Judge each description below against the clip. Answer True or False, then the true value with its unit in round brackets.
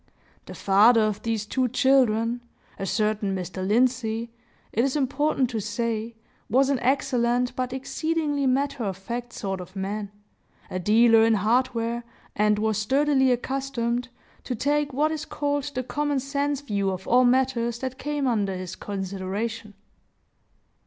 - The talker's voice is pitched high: True (240 Hz)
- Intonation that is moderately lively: True (3.9 semitones)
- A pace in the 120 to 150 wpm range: True (145 wpm)